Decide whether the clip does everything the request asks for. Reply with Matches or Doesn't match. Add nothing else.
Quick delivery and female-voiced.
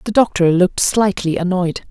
Doesn't match